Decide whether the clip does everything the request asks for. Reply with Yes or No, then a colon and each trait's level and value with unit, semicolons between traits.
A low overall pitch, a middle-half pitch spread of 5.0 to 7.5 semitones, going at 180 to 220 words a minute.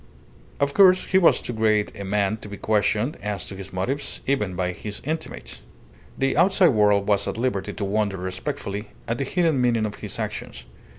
Yes: low, 105 Hz; average, 5.3 semitones; average, 190 wpm